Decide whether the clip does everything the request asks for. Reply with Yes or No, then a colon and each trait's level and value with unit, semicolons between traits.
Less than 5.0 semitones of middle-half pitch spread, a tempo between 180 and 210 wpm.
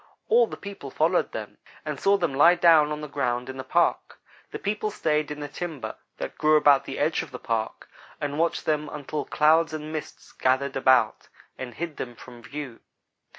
Yes: average, 3.6 semitones; average, 195 wpm